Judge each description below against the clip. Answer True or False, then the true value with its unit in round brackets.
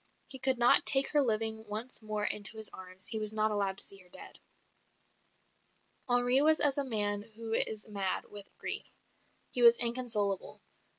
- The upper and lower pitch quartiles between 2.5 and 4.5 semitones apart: True (3.1 semitones)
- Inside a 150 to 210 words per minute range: True (175 wpm)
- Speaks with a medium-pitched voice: False (220 Hz)